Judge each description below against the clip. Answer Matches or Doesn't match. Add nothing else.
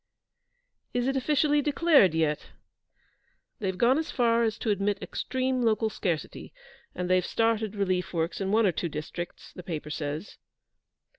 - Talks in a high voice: Matches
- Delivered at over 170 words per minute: Doesn't match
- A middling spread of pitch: Doesn't match